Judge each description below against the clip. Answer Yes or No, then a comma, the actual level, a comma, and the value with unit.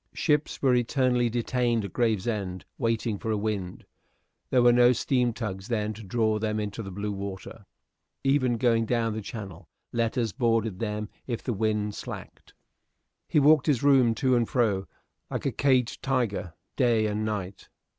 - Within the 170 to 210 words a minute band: No, average, 160 wpm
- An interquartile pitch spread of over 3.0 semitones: No, average, 2.7 semitones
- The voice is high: No, low, 115 Hz